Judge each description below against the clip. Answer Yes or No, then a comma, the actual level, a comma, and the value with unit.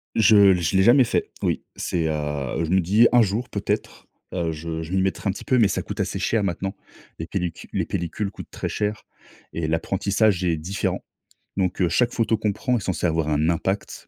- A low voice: Yes, very low, 95 Hz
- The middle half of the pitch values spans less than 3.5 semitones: No, average, 4.2 semitones